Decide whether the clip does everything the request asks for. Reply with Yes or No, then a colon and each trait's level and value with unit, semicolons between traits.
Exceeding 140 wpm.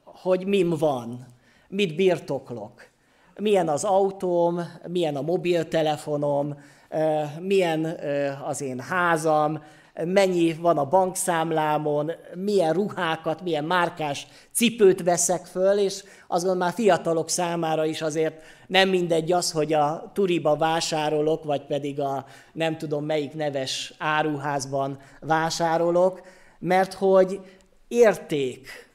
No: average, 110 wpm